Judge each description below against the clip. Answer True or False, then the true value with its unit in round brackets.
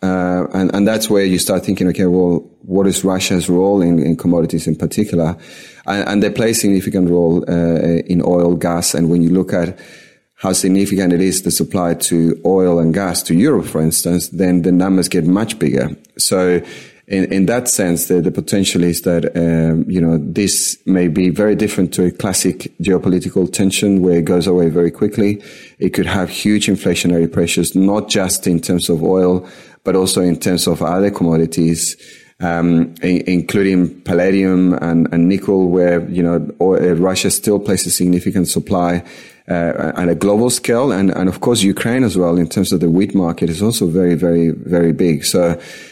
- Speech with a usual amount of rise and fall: False (2.0 semitones)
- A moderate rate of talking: True (190 wpm)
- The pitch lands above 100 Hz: False (90 Hz)